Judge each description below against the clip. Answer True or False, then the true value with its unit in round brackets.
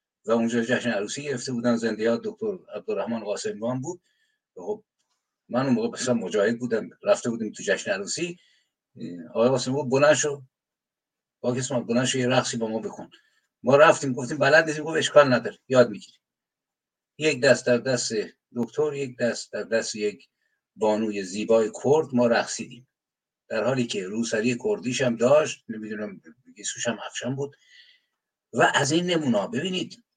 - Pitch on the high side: False (125 Hz)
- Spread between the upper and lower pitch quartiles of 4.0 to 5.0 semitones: True (4.4 semitones)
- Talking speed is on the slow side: False (145 wpm)